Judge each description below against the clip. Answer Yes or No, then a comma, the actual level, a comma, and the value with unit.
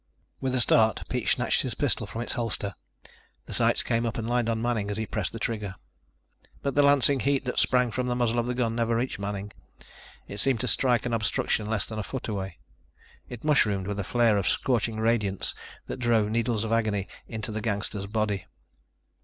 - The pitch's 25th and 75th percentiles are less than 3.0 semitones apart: Yes, narrow, 2.6 semitones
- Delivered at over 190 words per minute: Yes, fast, 205 wpm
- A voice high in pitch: No, low, 115 Hz